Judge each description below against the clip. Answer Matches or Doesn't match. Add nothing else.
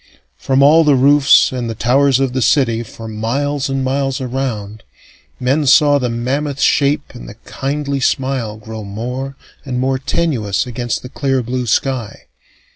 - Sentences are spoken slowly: Doesn't match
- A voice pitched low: Matches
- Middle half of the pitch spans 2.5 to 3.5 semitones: Matches